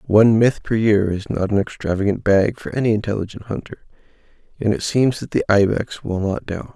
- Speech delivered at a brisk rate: No, average, 195 wpm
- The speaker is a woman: No, male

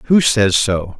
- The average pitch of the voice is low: Yes, low, 110 Hz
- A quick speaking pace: No, average, 180 wpm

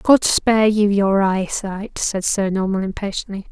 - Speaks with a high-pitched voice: Yes, high, 200 Hz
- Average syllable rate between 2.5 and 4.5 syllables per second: Yes, 4.4 syllables/s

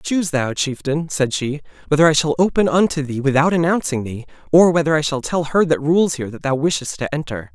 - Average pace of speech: No, fast, 225 wpm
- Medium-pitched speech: Yes, medium, 150 Hz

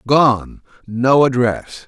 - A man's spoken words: Yes, male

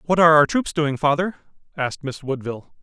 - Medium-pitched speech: Yes, medium, 150 Hz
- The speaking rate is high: No, average, 190 wpm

